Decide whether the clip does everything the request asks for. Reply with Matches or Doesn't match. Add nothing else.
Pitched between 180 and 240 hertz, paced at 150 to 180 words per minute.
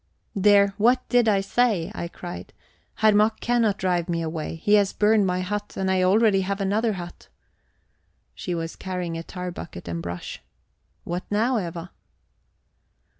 Matches